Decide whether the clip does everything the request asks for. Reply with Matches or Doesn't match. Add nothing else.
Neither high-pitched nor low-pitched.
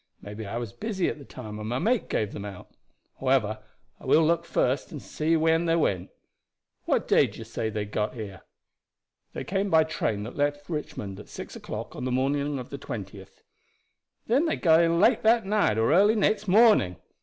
Matches